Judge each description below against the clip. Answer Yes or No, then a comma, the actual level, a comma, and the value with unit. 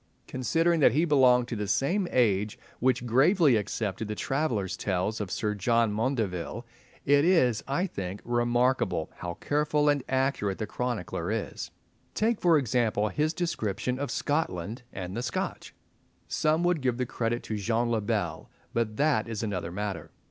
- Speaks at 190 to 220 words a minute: No, average, 160 wpm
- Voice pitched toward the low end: Yes, low, 120 Hz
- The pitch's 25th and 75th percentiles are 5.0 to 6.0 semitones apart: Yes, average, 5.3 semitones